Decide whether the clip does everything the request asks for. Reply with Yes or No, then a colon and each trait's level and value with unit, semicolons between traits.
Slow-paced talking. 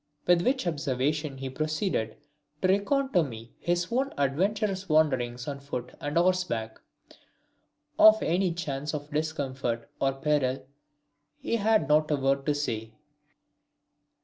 Yes: slow, 130 wpm